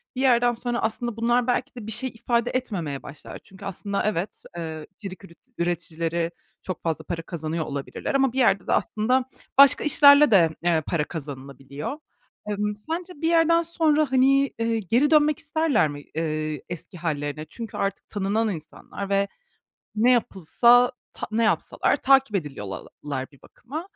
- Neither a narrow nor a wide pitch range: No, wide, 7.7 semitones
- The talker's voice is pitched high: Yes, high, 210 Hz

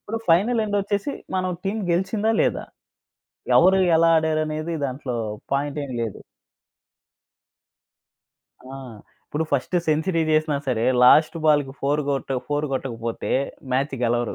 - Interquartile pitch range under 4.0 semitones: No, average, 5.2 semitones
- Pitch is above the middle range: No, medium, 155 Hz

